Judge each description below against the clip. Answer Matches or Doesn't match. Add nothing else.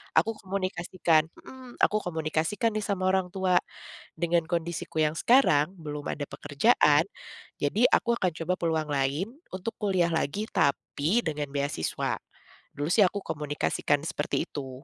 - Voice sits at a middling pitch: Matches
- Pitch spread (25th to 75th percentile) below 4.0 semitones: Doesn't match